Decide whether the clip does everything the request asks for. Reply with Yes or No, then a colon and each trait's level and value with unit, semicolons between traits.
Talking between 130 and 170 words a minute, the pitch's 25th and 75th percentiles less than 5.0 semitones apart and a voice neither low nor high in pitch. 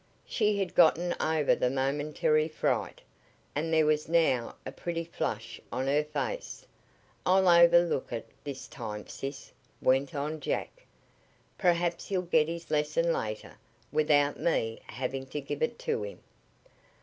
Yes: average, 140 wpm; average, 4.0 semitones; medium, 155 Hz